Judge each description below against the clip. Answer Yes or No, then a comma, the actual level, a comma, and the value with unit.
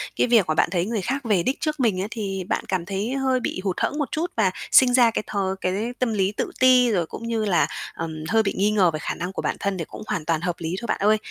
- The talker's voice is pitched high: Yes, high, 205 Hz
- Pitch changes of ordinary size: Yes, average, 4.8 semitones